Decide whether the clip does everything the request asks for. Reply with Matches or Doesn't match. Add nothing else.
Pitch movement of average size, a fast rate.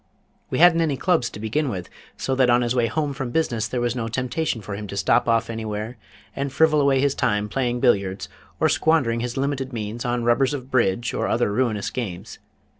Matches